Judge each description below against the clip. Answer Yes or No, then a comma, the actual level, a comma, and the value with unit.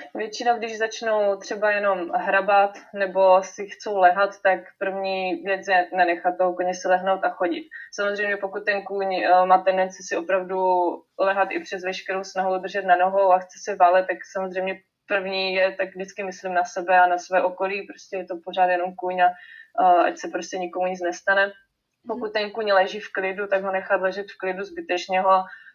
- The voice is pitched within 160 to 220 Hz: Yes, high, 190 Hz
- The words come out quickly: Yes, fast, 185 wpm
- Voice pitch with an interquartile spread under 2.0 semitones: Yes, narrow, 1.4 semitones